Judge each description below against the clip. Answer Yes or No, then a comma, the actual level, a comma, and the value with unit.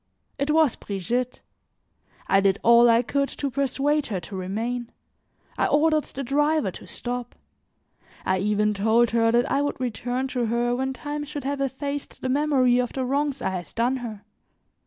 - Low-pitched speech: No, very high, 250 Hz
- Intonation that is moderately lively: Yes, average, 3.5 semitones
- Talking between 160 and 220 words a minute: Yes, average, 175 wpm